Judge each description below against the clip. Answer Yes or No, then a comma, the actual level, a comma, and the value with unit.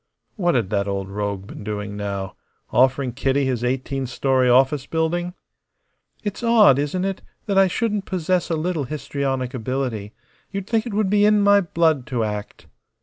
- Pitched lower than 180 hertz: Yes, low, 135 Hz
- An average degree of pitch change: No, wide, 7.3 semitones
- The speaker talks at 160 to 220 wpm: Yes, average, 170 wpm